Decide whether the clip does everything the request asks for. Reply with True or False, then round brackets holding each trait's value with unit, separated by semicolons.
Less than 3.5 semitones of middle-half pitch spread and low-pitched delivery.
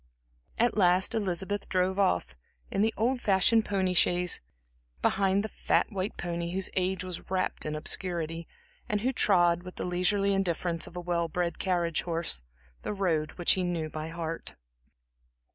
False (2.5 semitones; 180 Hz)